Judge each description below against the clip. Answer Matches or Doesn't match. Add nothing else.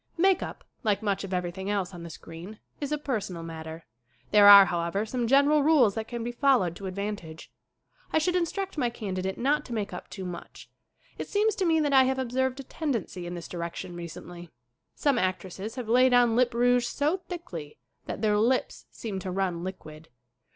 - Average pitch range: Doesn't match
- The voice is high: Matches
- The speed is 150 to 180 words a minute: Doesn't match